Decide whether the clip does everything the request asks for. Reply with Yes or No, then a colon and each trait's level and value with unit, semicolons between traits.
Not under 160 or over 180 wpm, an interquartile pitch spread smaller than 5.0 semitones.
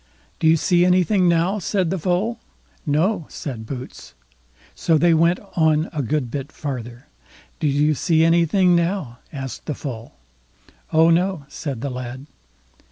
No: average, 150 wpm; average, 4.2 semitones